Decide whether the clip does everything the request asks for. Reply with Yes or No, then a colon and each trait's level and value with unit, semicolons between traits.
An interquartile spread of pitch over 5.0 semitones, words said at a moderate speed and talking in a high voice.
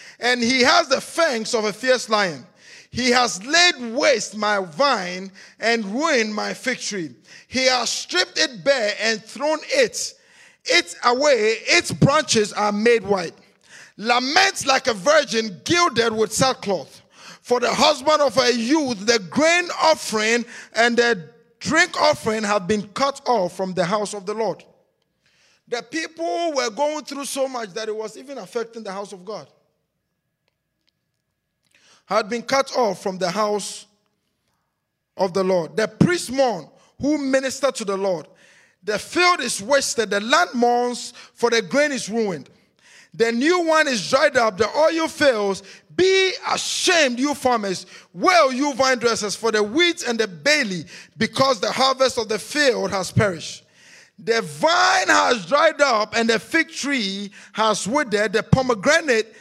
Yes: wide, 5.5 semitones; average, 155 wpm; high, 235 Hz